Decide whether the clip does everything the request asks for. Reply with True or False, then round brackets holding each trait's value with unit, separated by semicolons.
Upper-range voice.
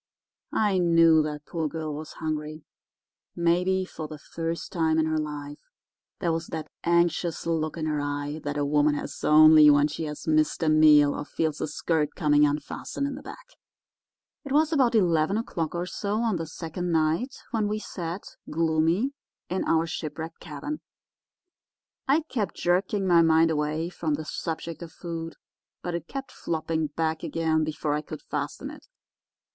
False (160 Hz)